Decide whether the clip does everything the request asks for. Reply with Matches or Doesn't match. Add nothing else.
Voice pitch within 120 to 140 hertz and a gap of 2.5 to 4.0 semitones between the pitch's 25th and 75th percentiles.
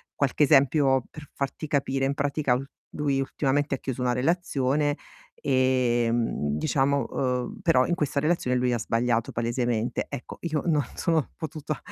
Matches